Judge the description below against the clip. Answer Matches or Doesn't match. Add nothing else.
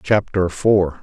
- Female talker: Doesn't match